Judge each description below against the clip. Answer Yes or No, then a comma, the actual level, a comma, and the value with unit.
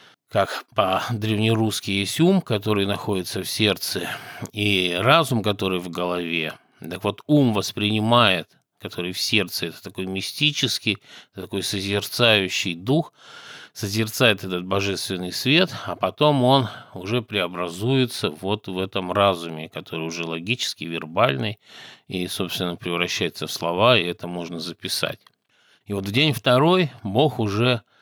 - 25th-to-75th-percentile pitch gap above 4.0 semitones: Yes, average, 4.8 semitones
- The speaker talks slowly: No, average, 125 wpm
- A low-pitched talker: Yes, low, 100 Hz